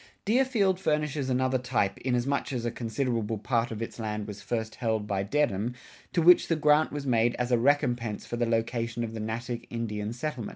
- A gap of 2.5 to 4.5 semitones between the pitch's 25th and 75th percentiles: Yes, average, 3.9 semitones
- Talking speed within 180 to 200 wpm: Yes, average, 195 wpm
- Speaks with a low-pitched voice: Yes, low, 120 Hz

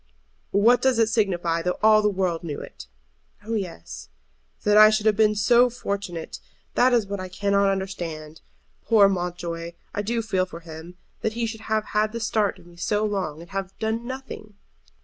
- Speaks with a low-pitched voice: No, high, 200 Hz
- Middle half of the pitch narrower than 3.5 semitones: No, average, 3.8 semitones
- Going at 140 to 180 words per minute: No, average, 190 wpm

